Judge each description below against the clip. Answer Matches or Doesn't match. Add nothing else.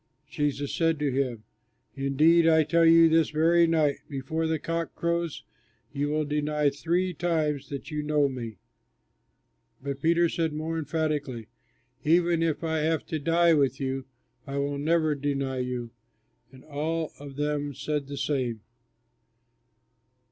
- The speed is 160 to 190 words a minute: Doesn't match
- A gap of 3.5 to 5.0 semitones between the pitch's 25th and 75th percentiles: Doesn't match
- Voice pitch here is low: Doesn't match